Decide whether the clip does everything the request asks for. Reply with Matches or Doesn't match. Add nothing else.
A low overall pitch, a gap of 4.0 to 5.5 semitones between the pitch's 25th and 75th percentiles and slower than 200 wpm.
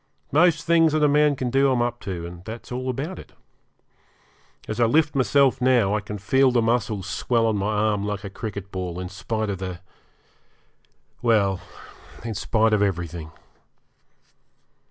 Matches